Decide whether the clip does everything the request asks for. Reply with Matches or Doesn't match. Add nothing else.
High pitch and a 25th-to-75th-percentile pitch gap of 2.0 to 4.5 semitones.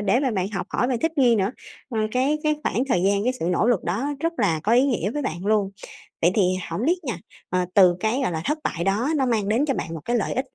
Doesn't match